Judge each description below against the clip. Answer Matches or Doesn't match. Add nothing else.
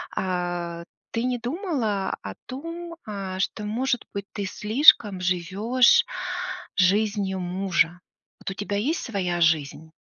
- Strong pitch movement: Doesn't match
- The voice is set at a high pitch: Matches